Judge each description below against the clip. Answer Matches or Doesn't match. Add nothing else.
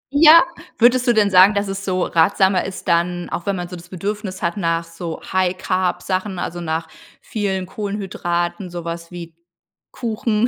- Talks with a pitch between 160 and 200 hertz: Matches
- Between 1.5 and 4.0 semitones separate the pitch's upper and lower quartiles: Matches